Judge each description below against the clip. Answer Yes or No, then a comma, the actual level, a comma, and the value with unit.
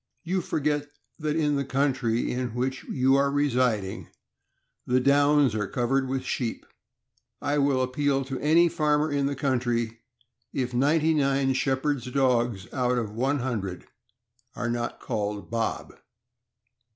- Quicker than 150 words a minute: No, average, 140 wpm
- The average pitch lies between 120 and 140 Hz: Yes, low, 135 Hz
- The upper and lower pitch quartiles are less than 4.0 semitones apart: Yes, average, 2.9 semitones